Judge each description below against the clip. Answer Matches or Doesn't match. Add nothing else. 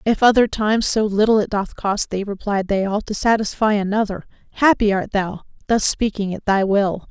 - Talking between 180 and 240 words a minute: Matches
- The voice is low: Doesn't match